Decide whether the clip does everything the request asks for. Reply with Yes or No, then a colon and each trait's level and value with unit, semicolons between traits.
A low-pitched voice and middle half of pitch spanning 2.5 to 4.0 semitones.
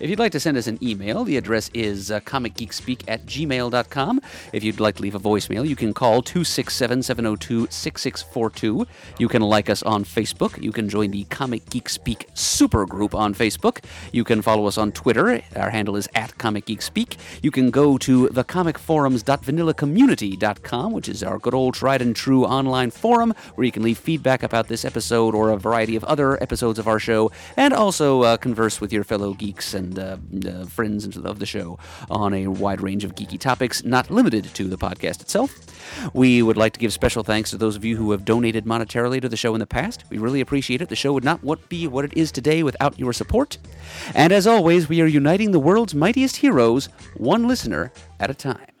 No: low, 115 Hz; average, 4.4 semitones